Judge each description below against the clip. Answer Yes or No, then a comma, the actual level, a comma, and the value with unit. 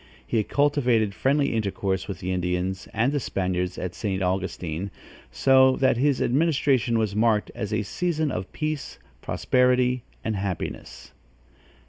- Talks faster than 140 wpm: No, slow, 135 wpm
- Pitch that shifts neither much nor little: No, wide, 5.7 semitones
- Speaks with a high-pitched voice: No, low, 110 Hz